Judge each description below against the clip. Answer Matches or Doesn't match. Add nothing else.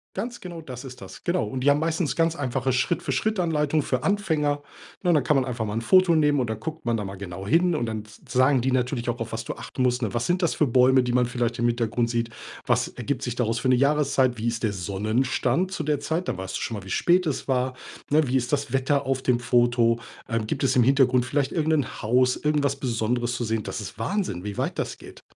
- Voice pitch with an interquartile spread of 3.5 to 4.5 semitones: Matches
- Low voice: Matches